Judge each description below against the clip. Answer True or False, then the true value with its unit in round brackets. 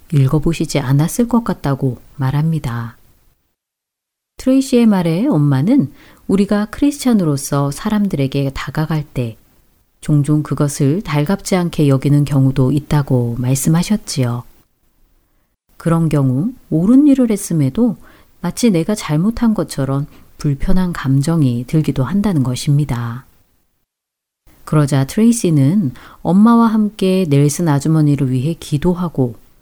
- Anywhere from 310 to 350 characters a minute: False (270 characters per minute)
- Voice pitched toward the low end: False (150 Hz)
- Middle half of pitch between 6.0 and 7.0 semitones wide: False (5.5 semitones)